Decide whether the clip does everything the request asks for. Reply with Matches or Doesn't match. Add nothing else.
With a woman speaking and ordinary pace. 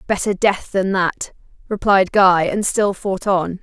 Matches